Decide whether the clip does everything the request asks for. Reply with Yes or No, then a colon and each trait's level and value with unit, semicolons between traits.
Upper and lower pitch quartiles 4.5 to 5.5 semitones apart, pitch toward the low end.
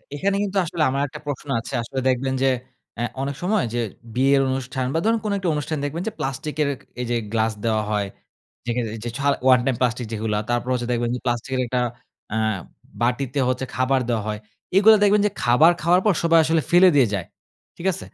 Yes: average, 5.1 semitones; low, 130 Hz